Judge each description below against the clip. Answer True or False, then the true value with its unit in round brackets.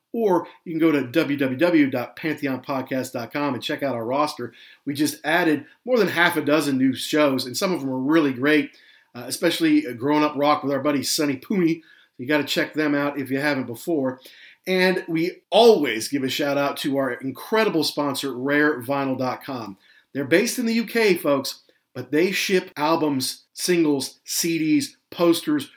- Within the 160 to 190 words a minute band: True (170 wpm)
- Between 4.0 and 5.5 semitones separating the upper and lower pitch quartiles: False (3.6 semitones)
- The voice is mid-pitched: True (150 Hz)